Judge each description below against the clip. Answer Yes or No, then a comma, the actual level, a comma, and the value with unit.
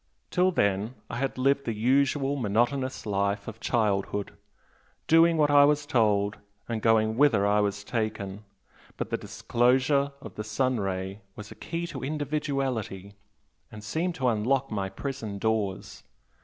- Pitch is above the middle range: No, low, 115 Hz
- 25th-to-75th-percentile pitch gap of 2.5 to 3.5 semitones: No, average, 5.1 semitones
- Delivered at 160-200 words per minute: No, average, 150 wpm